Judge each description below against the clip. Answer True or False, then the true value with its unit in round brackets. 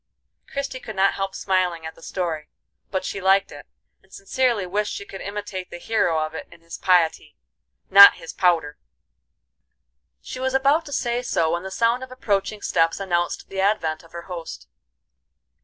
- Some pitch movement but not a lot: True (4.0 semitones)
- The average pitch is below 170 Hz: False (190 Hz)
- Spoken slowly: False (175 wpm)